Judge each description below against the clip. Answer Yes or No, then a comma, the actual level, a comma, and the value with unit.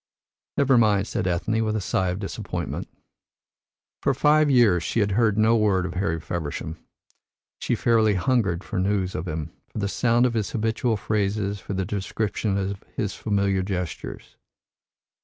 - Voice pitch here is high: No, low, 100 Hz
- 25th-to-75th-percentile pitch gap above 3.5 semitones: No, average, 3.1 semitones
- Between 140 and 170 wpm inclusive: Yes, average, 160 wpm